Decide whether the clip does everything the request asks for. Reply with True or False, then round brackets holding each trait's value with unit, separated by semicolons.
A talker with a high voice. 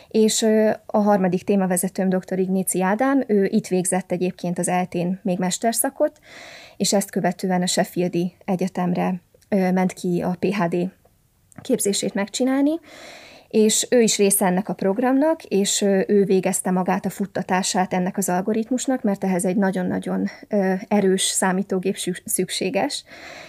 True (195 Hz)